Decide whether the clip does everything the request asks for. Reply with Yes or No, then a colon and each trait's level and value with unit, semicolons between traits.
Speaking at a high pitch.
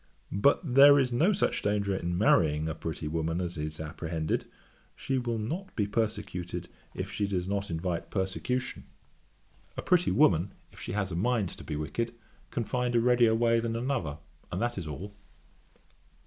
No: low, 105 Hz